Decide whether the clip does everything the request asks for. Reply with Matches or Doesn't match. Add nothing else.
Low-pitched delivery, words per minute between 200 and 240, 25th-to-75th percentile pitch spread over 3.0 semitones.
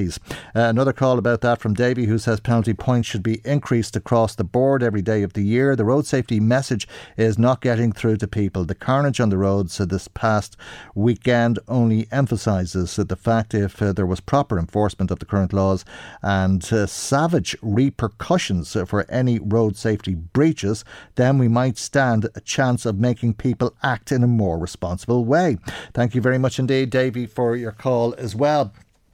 Doesn't match